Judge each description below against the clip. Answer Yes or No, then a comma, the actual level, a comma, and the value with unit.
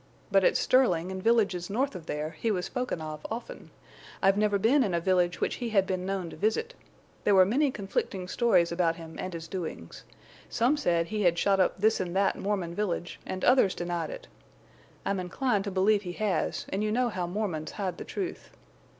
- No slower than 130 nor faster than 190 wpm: No, fast, 205 wpm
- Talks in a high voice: Yes, high, 195 Hz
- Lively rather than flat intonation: No, average, 3.7 semitones